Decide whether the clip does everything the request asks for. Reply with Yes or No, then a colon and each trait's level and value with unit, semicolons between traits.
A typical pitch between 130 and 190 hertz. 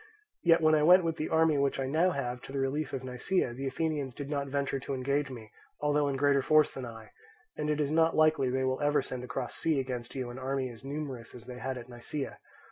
Yes: medium, 140 Hz